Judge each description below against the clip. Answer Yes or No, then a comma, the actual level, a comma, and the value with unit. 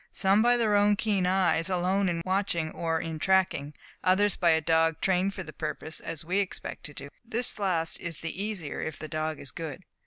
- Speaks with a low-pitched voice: No, medium, 180 Hz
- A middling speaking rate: No, fast, 210 wpm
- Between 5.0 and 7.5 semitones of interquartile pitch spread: No, average, 3.5 semitones